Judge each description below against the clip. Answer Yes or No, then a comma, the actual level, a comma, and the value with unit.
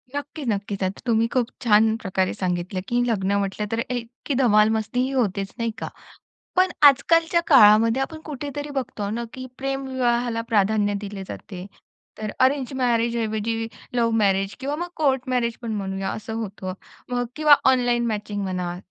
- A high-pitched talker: Yes, high, 230 Hz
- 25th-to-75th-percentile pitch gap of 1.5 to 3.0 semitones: No, average, 4.1 semitones